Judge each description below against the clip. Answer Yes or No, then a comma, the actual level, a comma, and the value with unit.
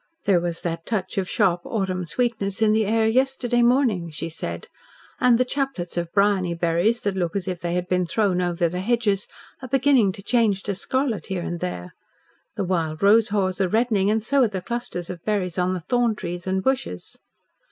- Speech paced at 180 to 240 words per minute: Yes, fast, 205 wpm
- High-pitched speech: Yes, high, 195 Hz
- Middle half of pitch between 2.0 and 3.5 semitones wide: No, average, 4.4 semitones